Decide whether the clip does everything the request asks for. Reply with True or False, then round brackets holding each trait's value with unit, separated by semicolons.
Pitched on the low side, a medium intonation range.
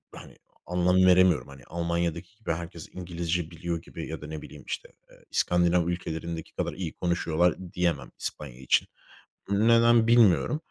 False (85 Hz; 1.8 semitones)